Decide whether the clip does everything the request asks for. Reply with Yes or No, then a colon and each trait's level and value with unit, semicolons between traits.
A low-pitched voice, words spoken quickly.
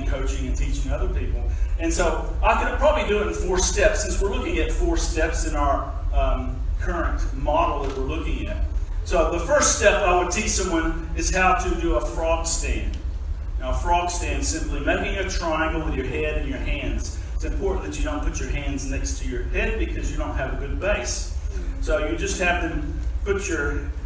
Yes: very low, 75 Hz; fast, 210 wpm